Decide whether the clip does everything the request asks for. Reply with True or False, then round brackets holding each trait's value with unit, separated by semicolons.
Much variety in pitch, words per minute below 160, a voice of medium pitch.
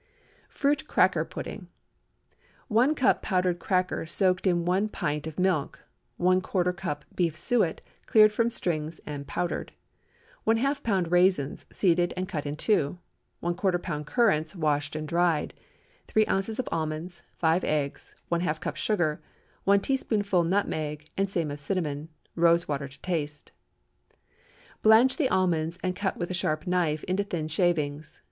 False (3.9 semitones; 140 wpm; 175 Hz)